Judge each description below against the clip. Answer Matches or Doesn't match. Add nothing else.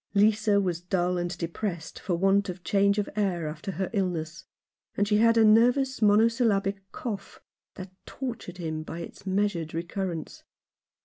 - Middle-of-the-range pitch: Doesn't match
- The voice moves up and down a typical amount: Matches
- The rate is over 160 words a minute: Doesn't match